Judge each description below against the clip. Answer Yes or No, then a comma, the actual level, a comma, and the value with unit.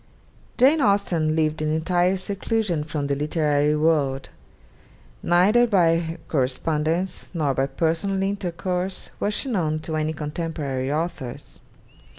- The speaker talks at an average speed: No, slow, 120 wpm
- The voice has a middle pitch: Yes, medium, 165 Hz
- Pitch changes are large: No, average, 3.7 semitones